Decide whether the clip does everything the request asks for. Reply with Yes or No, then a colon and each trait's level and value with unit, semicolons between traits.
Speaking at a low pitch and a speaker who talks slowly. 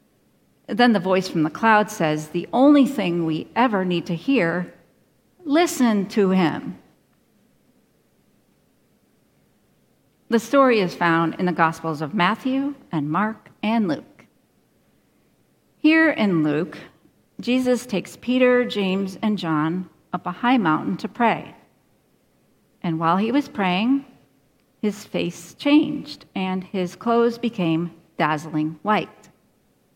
No: high, 195 Hz; slow, 120 wpm